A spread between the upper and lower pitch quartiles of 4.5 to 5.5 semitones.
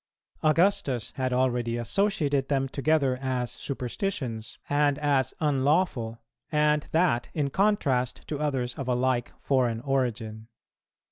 No: average, 3.4 semitones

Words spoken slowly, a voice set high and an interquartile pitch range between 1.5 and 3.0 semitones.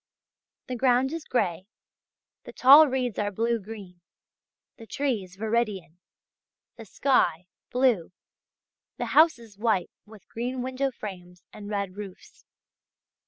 No: slow, 120 wpm; high, 225 Hz; average, 4.8 semitones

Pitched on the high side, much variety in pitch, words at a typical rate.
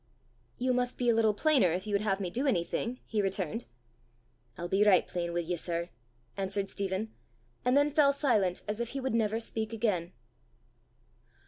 No: high, 210 Hz; average, 4.5 semitones; average, 185 wpm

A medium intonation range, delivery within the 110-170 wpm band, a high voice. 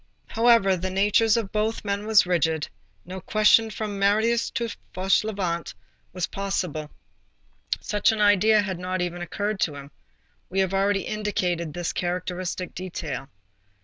Yes: average, 3.1 semitones; average, 145 wpm; high, 195 Hz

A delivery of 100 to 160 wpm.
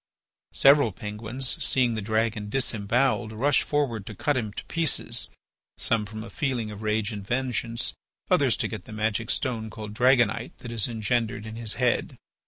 No: average, 170 wpm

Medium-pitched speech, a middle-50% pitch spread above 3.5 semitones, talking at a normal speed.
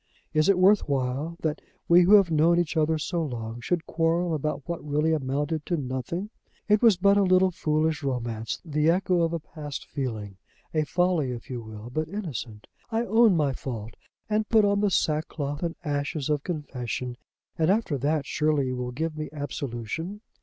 Yes: medium, 155 Hz; average, 4.5 semitones; average, 185 wpm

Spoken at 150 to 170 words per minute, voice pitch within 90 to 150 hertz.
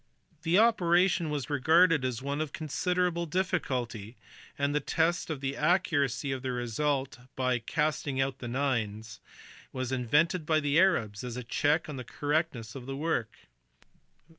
Yes: average, 155 wpm; medium, 140 Hz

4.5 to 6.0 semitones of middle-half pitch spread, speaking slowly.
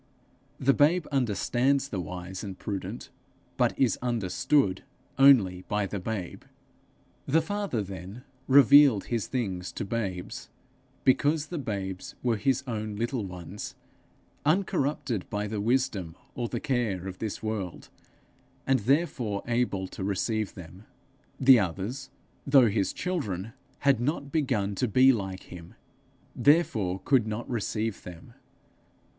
Yes: wide, 5.6 semitones; slow, 130 wpm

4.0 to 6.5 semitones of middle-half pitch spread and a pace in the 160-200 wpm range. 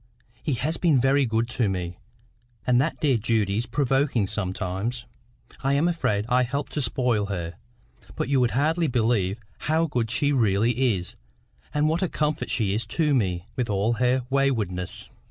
Yes: average, 5.1 semitones; average, 170 wpm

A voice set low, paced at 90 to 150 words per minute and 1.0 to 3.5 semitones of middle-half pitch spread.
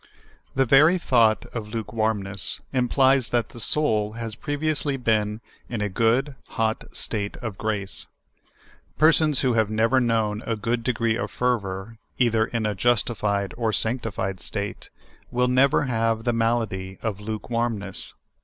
Yes: low, 115 Hz; average, 145 wpm; average, 2.7 semitones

